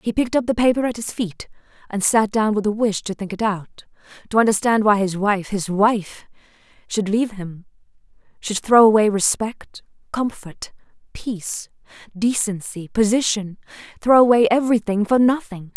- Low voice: No, high, 215 Hz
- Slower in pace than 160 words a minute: Yes, average, 150 wpm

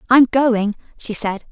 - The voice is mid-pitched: No, high, 230 Hz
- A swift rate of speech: No, average, 160 wpm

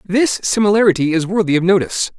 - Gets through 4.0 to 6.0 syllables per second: No, 6.4 syllables/s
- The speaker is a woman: No, male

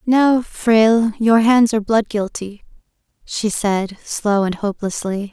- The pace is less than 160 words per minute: Yes, slow, 135 wpm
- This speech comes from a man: No, female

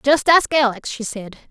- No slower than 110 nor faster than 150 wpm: No, average, 200 wpm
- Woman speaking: Yes, female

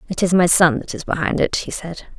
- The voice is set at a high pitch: No, medium, 170 Hz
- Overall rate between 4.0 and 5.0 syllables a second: No, 5.7 syllables/s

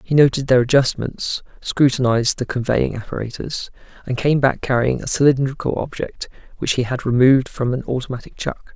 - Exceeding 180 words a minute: No, average, 160 wpm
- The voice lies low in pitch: Yes, low, 130 Hz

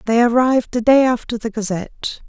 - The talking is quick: No, average, 185 wpm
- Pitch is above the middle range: Yes, high, 230 Hz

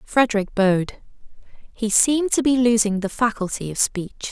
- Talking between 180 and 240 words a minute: No, average, 155 wpm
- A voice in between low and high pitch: No, high, 220 Hz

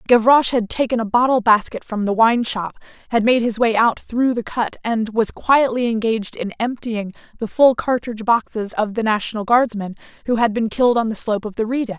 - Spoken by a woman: Yes, female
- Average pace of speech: No, fast, 225 wpm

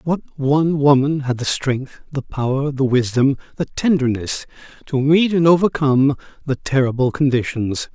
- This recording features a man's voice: Yes, male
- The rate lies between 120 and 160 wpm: Yes, average, 145 wpm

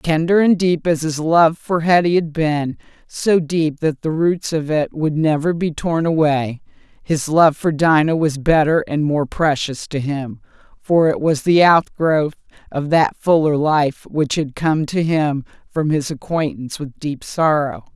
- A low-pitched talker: No, medium, 155 Hz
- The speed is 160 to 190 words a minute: Yes, average, 170 wpm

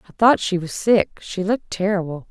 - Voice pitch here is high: Yes, high, 195 Hz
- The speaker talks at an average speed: Yes, average, 180 wpm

